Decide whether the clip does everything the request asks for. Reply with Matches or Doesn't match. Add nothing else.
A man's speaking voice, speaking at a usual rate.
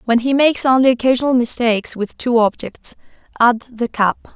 Doesn't match